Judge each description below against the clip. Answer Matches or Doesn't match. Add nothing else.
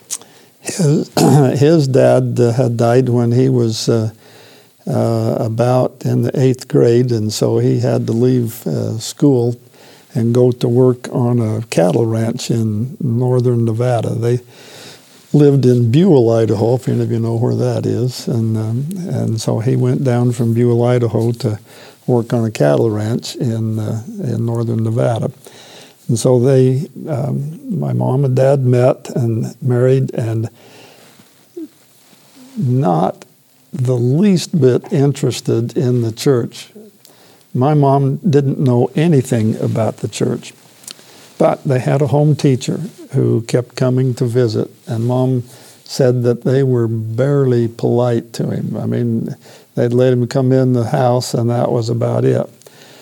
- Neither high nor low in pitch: Doesn't match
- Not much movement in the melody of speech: Matches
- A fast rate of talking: Doesn't match